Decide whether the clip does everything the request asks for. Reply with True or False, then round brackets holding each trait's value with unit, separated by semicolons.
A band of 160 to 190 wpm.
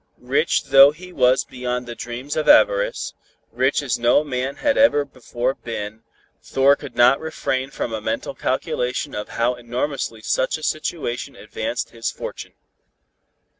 False (150 wpm)